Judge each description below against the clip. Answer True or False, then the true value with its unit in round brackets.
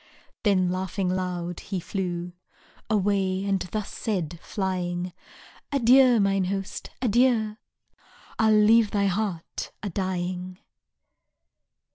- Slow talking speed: True (100 wpm)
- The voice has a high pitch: True (195 Hz)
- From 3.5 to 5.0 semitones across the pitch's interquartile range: False (2.8 semitones)